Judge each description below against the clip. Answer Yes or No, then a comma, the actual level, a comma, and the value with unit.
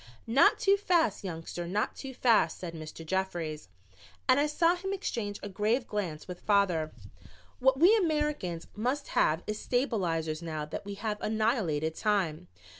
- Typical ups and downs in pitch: No, wide, 7.8 semitones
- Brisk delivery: No, average, 155 wpm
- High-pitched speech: Yes, high, 205 Hz